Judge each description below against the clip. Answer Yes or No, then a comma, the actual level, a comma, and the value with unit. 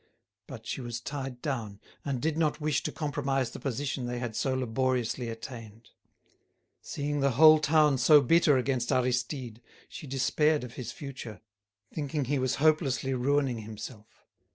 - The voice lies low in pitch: Yes, low, 130 Hz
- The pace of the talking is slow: No, average, 155 wpm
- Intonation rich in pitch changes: No, average, 3.1 semitones